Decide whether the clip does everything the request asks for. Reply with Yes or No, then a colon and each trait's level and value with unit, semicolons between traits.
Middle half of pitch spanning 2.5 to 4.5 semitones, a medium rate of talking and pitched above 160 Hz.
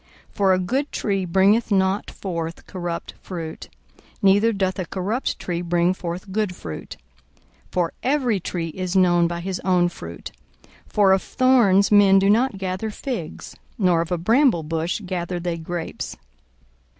Yes: average, 2.8 semitones; average, 160 wpm; medium, 185 Hz